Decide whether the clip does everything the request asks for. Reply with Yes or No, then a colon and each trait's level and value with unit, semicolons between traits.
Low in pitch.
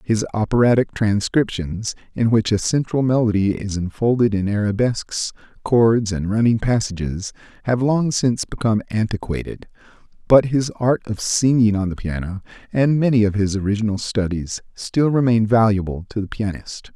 Yes: low, 110 Hz